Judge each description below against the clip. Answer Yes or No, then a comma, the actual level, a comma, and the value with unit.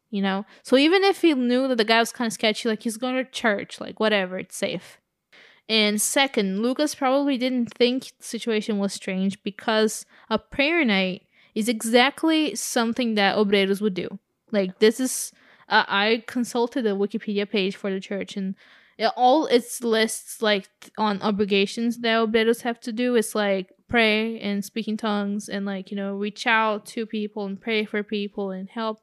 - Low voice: No, high, 220 Hz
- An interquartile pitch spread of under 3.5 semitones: Yes, average, 2.8 semitones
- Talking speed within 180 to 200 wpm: Yes, average, 185 wpm